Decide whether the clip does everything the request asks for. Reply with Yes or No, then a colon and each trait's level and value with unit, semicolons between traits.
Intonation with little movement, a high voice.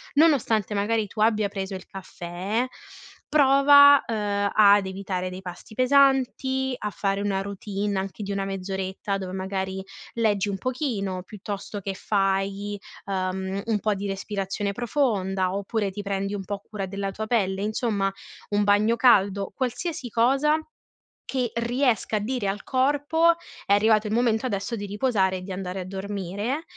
No: average, 3.2 semitones; high, 205 Hz